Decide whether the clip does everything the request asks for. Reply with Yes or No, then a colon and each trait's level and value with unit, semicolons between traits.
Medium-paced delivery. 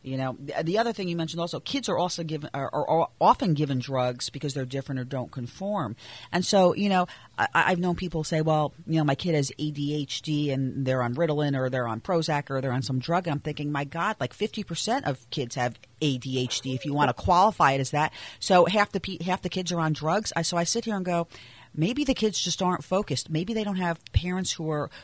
No: fast, 265 wpm